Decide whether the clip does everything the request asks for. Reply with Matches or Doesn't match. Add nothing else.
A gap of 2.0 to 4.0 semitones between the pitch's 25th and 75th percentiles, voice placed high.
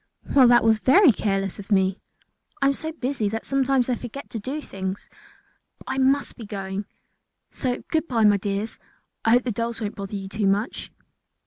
Doesn't match